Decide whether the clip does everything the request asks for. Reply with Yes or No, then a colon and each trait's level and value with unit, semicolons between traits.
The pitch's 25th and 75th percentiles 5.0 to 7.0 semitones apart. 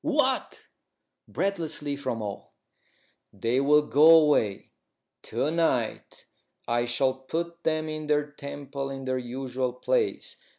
No: average, 3.6 semitones